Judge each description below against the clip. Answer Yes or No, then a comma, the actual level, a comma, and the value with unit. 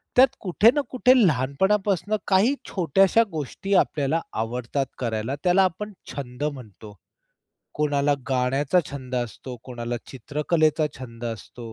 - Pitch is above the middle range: No, medium, 145 Hz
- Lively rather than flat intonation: Yes, wide, 6.9 semitones